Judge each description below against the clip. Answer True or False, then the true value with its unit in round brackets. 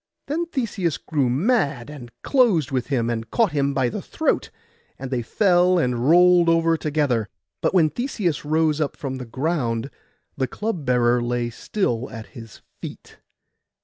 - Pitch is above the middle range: False (145 Hz)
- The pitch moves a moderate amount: False (6.2 semitones)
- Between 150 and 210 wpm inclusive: True (160 wpm)